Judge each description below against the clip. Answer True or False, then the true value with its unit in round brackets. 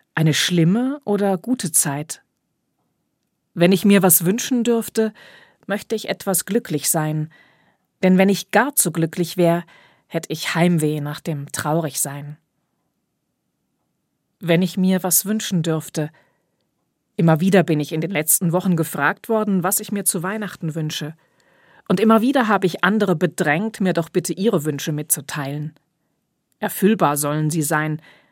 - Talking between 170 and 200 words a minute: False (145 wpm)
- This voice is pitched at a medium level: True (175 Hz)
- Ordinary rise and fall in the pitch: True (4.2 semitones)